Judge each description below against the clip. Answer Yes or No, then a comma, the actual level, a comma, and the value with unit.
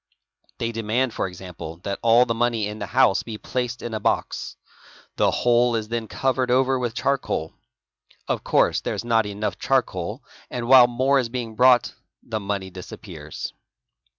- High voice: No, low, 115 Hz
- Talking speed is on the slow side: No, average, 170 wpm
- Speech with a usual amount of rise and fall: Yes, average, 3.3 semitones